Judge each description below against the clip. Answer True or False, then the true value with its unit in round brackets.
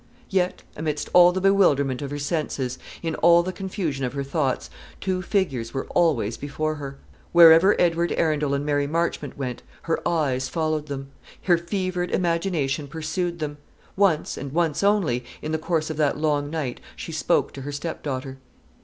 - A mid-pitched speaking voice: True (155 Hz)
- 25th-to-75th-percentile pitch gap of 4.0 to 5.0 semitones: False (3.5 semitones)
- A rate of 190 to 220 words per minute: False (170 wpm)